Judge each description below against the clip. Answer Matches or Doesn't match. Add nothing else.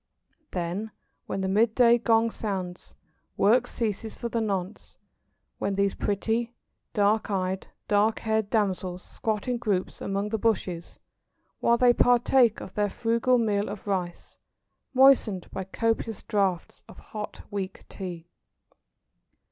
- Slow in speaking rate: Matches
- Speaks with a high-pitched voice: Matches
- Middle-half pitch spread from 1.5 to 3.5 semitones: Matches